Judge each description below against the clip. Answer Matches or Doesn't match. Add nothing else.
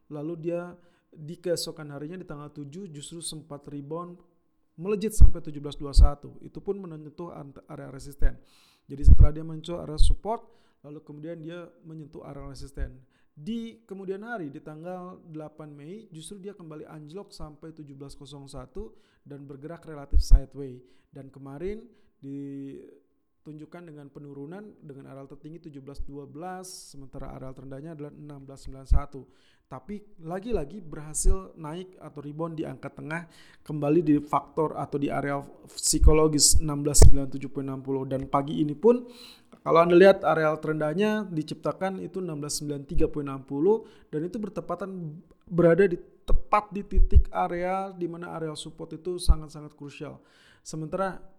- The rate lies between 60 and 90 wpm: Doesn't match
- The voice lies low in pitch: Doesn't match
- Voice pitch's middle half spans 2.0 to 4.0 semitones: Matches